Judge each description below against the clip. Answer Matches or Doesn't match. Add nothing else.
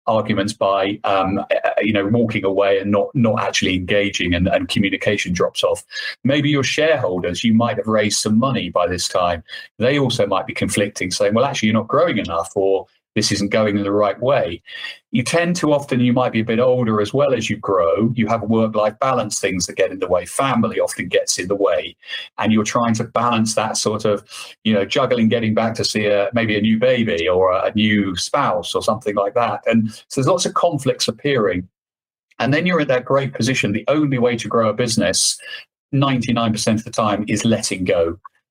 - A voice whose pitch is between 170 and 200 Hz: Doesn't match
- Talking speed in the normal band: Doesn't match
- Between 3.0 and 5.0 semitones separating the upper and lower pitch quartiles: Matches